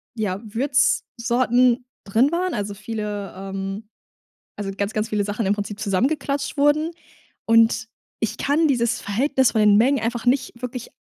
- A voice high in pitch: Yes, high, 230 Hz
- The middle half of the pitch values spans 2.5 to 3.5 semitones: No, average, 4.1 semitones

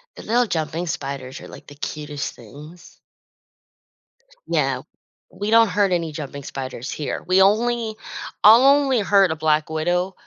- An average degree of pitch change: No, wide, 6.0 semitones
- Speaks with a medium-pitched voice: Yes, medium, 175 Hz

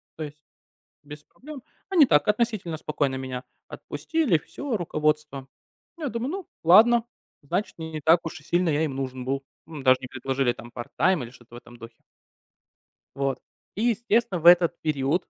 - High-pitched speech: No, medium, 155 Hz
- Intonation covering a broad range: Yes, wide, 7.0 semitones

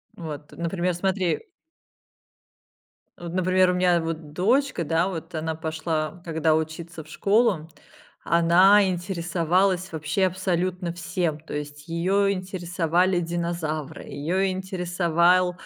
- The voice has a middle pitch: Yes, medium, 175 Hz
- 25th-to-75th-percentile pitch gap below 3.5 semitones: Yes, narrow, 2.4 semitones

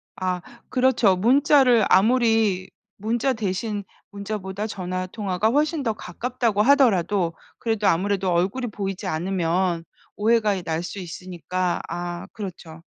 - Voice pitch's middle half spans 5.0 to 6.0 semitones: No, average, 3.7 semitones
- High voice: Yes, high, 200 Hz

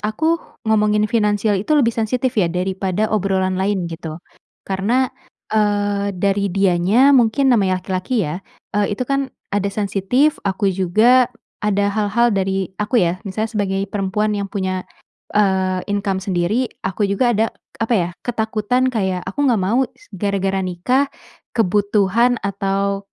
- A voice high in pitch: Yes, high, 205 Hz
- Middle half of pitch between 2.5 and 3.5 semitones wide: Yes, average, 2.9 semitones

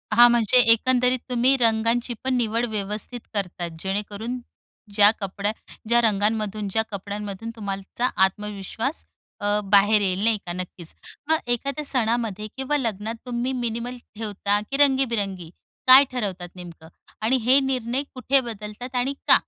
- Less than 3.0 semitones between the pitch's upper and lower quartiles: No, average, 3.6 semitones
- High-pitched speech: Yes, high, 225 Hz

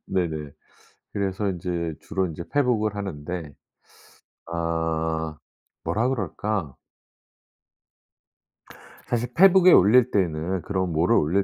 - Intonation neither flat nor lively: Yes, average, 4.7 semitones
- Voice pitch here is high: No, very low, 95 Hz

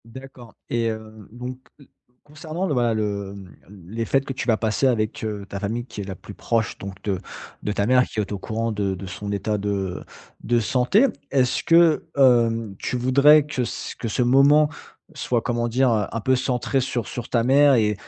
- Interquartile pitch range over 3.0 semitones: Yes, average, 3.8 semitones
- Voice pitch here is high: No, low, 115 Hz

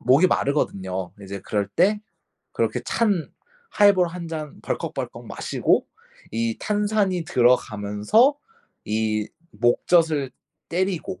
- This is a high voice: No, medium, 150 Hz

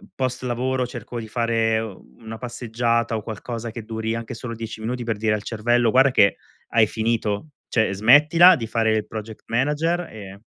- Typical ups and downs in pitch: No, narrow, 2.0 semitones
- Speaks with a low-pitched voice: Yes, low, 115 Hz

